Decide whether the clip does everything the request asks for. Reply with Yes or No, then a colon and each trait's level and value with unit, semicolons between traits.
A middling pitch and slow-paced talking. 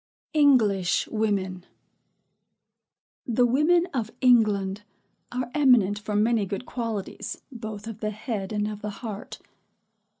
No: high, 215 Hz; slow, 120 wpm